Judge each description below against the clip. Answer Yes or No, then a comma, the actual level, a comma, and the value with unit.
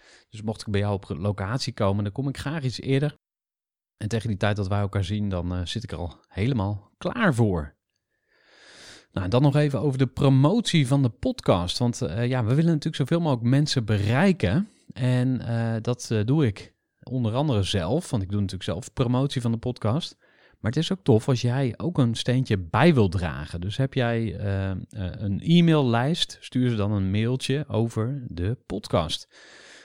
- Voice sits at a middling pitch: No, low, 120 Hz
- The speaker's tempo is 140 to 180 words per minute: No, average, 195 wpm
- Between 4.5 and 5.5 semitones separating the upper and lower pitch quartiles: Yes, average, 5.0 semitones